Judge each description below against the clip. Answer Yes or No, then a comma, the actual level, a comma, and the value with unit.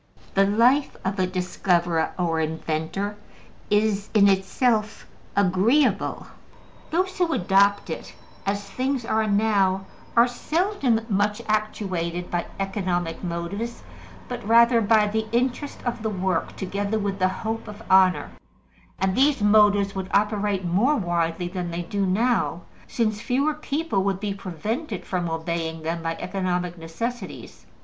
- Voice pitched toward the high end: Yes, high, 200 Hz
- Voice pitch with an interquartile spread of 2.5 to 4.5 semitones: Yes, average, 3.8 semitones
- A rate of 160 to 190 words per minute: No, slow, 135 wpm